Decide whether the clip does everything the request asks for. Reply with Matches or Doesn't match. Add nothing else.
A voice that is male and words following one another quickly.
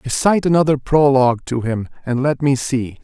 Doesn't match